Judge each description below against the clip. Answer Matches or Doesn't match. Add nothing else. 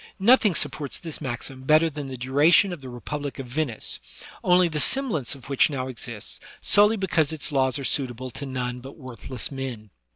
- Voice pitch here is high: Doesn't match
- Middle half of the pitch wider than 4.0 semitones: Doesn't match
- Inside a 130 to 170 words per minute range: Doesn't match